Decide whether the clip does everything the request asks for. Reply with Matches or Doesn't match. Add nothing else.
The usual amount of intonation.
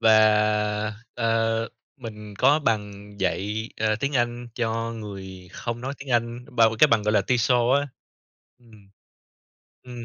Doesn't match